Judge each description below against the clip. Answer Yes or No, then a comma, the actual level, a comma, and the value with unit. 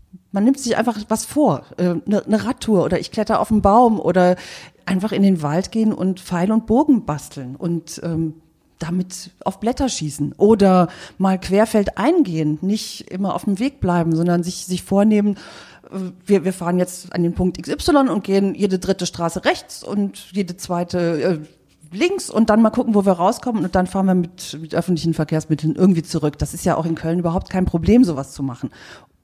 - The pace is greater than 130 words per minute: Yes, average, 185 wpm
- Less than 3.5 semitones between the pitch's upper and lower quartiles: No, average, 3.8 semitones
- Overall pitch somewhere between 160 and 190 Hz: Yes, medium, 185 Hz